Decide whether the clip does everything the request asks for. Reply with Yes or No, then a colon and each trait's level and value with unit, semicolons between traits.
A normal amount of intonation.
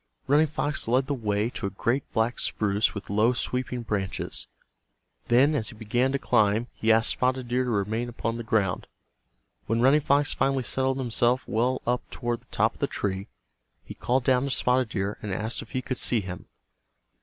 Yes: average, 3.0 semitones